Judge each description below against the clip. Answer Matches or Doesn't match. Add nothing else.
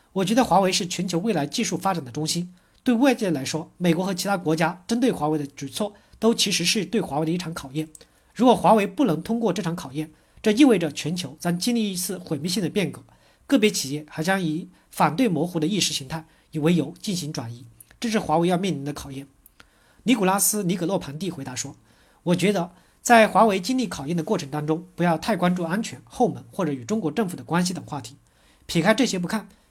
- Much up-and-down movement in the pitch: Doesn't match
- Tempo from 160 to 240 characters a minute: Doesn't match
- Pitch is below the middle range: Doesn't match